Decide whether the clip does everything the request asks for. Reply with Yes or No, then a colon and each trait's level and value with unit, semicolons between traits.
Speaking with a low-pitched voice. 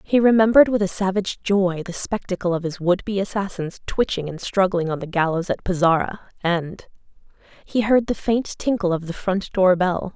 No: high, 190 Hz